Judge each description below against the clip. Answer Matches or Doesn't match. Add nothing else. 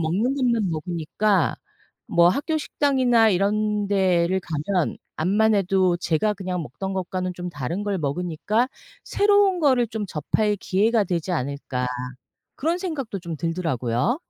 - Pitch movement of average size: Matches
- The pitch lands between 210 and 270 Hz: Doesn't match